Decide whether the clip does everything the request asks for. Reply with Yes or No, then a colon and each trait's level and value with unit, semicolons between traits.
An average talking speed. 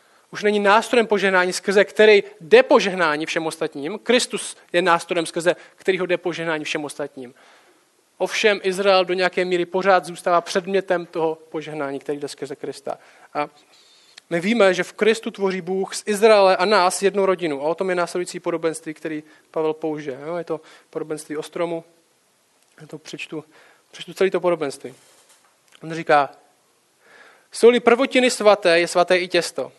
Yes: average, 150 wpm